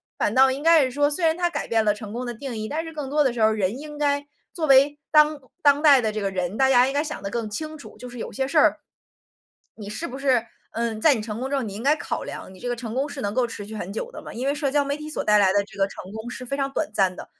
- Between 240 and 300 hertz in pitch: Yes, very high, 255 Hz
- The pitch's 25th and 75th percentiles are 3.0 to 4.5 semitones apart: No, average, 5.1 semitones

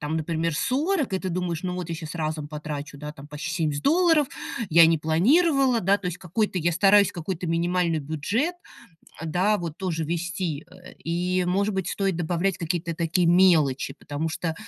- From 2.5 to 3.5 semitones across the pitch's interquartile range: Yes, average, 3.2 semitones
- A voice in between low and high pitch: Yes, medium, 175 Hz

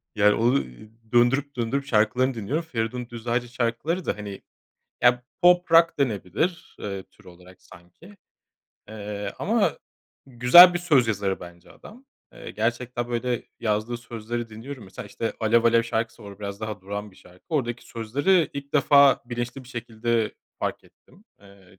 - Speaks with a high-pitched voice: No, low, 120 Hz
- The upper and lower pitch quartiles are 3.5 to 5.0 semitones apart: Yes, average, 4.1 semitones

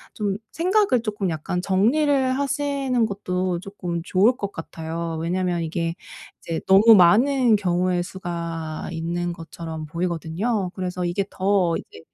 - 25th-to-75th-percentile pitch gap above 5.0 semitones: No, average, 4.4 semitones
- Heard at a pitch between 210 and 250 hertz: No, medium, 185 Hz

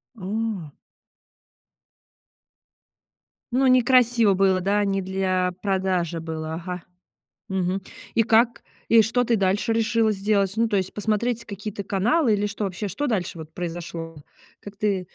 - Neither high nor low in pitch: No, high, 200 Hz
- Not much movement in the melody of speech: No, average, 3.4 semitones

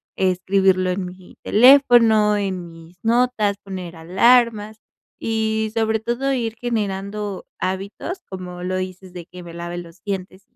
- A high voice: Yes, high, 195 Hz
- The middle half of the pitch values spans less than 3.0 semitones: No, average, 3.3 semitones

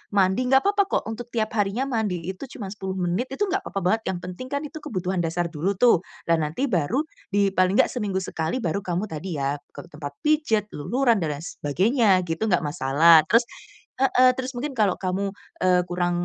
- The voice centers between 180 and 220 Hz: Yes, high, 190 Hz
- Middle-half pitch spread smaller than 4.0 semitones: No, wide, 5.6 semitones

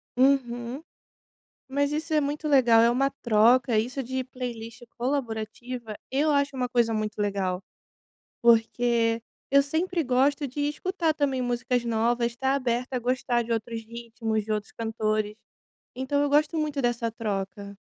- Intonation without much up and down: No, average, 3.4 semitones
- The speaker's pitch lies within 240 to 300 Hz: Yes, high, 245 Hz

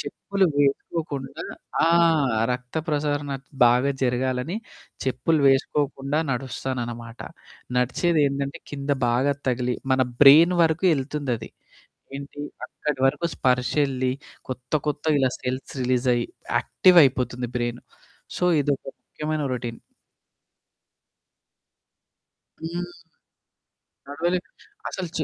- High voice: No, low, 135 Hz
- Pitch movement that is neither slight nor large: Yes, average, 3.1 semitones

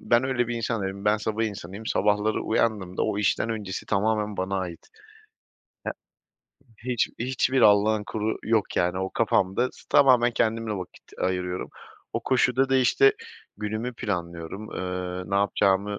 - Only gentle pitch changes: No, average, 3.2 semitones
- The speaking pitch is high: No, low, 105 Hz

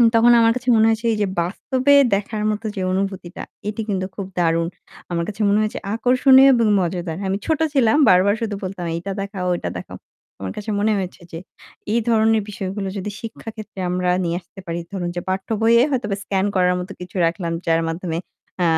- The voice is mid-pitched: No, high, 200 Hz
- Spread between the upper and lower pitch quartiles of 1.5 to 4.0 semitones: Yes, average, 3.7 semitones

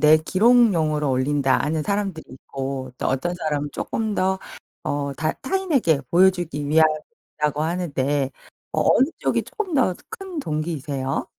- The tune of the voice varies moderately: Yes, average, 4.9 semitones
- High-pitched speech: No, medium, 155 Hz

